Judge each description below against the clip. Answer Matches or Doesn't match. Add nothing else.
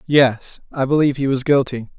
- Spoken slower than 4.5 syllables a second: Doesn't match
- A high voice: Doesn't match